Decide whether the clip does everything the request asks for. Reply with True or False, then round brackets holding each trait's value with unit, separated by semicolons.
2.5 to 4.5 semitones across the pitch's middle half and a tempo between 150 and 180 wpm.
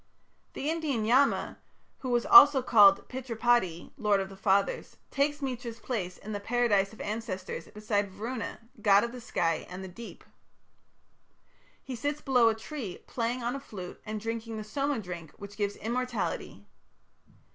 True (3.9 semitones; 155 wpm)